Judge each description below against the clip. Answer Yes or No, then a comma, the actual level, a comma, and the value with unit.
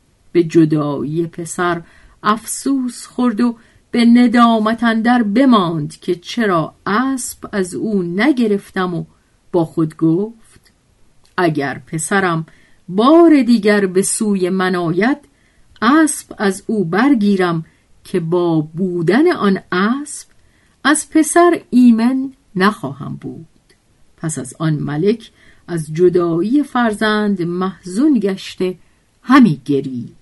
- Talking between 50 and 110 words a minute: Yes, slow, 105 wpm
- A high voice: Yes, high, 195 Hz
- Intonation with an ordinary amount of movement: No, wide, 5.8 semitones